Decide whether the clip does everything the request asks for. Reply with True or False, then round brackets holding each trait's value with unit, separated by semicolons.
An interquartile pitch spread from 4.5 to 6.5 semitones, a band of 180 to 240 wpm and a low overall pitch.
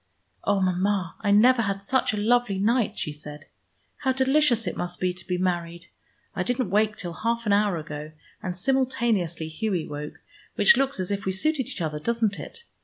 False (4.9 semitones; 190 wpm; 200 Hz)